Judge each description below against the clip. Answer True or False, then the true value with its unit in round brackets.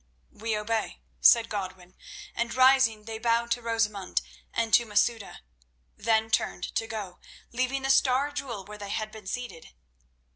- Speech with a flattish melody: True (2.3 semitones)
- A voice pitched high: True (225 Hz)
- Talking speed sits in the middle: True (150 wpm)